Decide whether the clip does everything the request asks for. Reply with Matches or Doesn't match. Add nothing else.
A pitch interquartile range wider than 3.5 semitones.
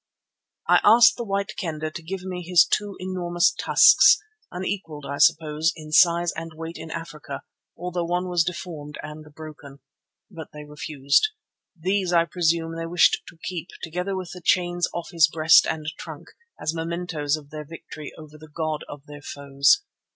Doesn't match